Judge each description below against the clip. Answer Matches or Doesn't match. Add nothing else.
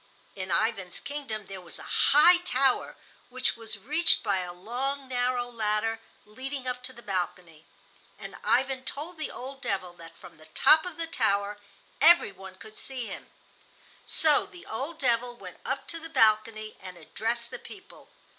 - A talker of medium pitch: Doesn't match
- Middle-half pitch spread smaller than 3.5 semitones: Doesn't match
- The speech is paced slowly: Doesn't match